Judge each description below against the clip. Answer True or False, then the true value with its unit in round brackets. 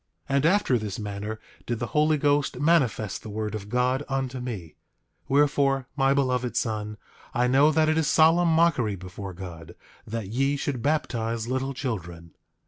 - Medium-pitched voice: False (125 Hz)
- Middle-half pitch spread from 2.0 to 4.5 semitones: False (5.0 semitones)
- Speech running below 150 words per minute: False (165 wpm)